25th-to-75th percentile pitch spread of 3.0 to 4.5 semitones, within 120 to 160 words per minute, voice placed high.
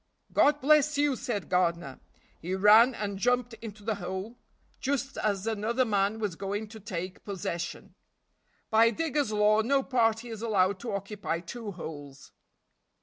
Yes: average, 3.9 semitones; average, 145 wpm; high, 215 Hz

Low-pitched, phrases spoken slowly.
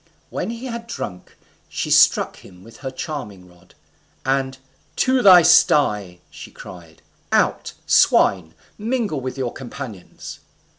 Yes: low, 130 Hz; slow, 130 wpm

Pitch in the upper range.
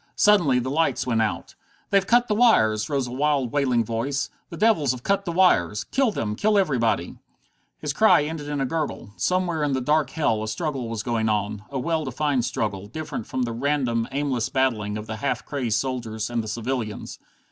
No: low, 130 Hz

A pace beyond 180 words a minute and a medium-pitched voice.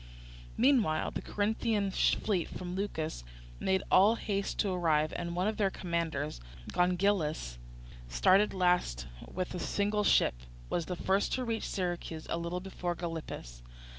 No: average, 140 wpm; medium, 180 Hz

